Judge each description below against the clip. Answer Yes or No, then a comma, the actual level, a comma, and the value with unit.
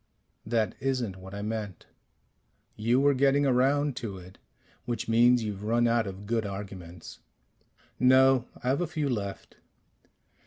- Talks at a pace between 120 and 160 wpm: Yes, average, 145 wpm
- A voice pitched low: Yes, low, 115 Hz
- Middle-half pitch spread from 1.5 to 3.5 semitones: No, average, 4.4 semitones